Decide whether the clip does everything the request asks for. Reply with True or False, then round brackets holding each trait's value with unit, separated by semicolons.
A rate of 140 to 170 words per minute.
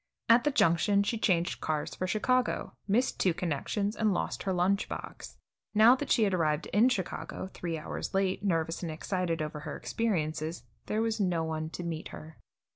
False (185 wpm)